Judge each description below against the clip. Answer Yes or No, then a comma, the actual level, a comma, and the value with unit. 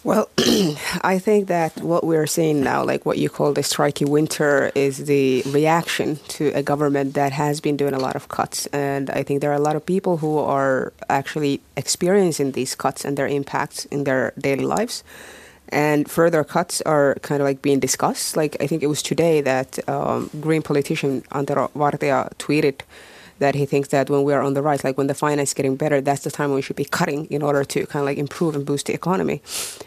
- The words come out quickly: Yes, fast, 220 wpm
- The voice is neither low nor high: Yes, medium, 145 Hz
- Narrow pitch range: Yes, narrow, 1.8 semitones